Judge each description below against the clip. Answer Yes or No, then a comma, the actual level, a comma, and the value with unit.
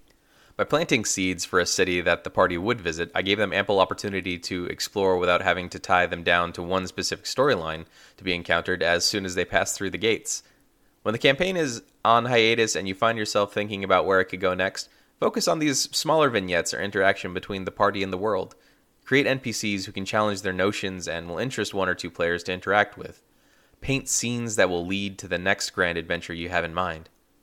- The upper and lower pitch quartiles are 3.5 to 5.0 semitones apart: No, average, 3.1 semitones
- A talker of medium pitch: No, very low, 95 Hz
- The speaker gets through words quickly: Yes, fast, 220 wpm